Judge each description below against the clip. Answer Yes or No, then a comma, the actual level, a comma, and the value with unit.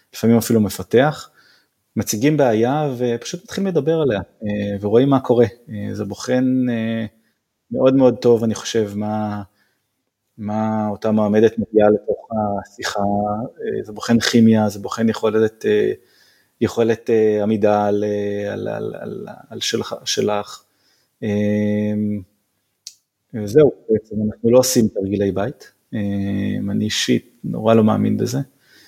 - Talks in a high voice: No, low, 110 Hz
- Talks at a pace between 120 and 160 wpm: No, average, 110 wpm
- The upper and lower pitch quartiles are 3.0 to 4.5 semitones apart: No, narrow, 2.4 semitones